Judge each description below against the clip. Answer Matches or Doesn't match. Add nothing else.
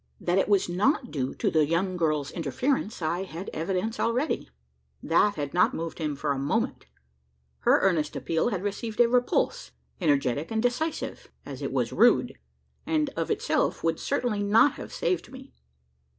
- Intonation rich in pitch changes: Matches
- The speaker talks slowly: Doesn't match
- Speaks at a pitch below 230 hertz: Matches